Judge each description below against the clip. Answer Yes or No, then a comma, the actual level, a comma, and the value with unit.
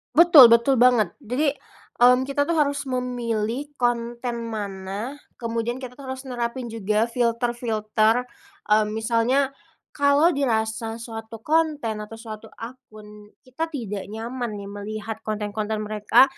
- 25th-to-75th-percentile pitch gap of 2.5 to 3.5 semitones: Yes, average, 3.1 semitones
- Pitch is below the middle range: No, high, 235 Hz